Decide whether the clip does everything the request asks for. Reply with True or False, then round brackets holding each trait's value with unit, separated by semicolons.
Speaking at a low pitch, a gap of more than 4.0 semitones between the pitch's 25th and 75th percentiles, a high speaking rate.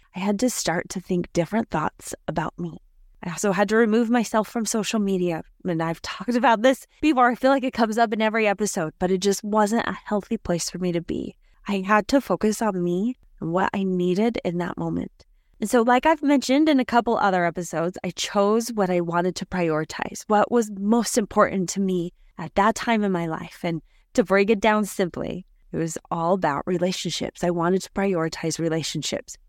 False (200 Hz; 4.4 semitones; 210 wpm)